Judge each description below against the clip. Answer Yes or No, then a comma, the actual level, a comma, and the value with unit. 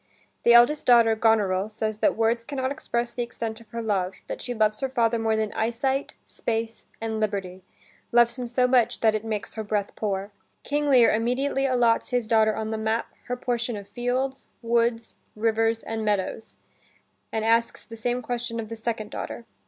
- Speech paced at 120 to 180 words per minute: No, average, 190 wpm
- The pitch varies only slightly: Yes, narrow, 1.8 semitones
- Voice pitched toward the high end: Yes, high, 230 Hz